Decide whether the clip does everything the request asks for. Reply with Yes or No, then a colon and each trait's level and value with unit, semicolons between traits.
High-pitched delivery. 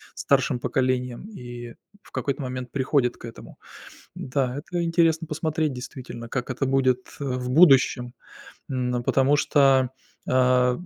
No: low, 130 Hz